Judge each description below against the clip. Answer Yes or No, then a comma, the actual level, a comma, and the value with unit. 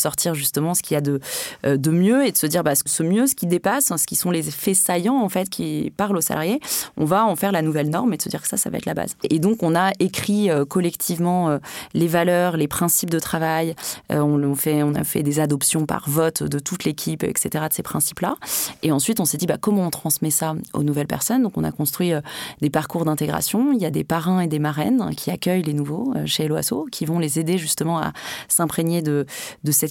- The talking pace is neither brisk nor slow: No, fast, 245 wpm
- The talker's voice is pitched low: No, medium, 165 Hz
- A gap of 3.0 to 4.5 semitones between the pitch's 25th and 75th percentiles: Yes, average, 3.4 semitones